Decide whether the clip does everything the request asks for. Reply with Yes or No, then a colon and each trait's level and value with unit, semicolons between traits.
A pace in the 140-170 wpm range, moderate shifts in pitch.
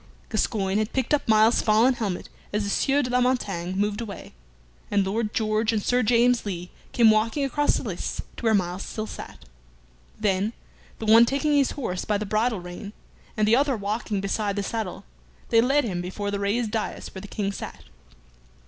No: average, 195 wpm; average, 3.0 semitones